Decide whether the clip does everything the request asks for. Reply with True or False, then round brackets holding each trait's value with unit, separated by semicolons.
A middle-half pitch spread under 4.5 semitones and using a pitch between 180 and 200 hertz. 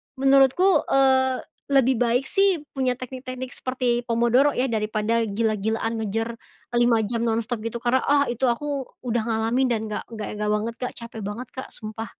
False (2.7 semitones; 240 Hz)